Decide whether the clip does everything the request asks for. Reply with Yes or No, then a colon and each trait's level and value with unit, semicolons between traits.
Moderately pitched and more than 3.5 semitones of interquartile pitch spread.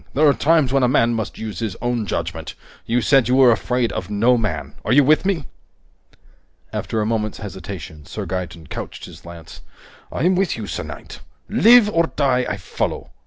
No: low, 120 Hz; average, 5.2 semitones